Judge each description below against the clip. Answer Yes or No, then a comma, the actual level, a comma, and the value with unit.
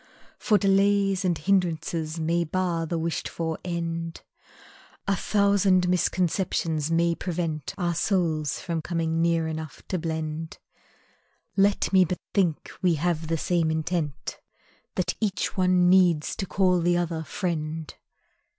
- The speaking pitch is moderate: Yes, medium, 170 Hz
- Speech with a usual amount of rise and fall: No, narrow, 2.3 semitones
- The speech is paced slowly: Yes, slow, 130 wpm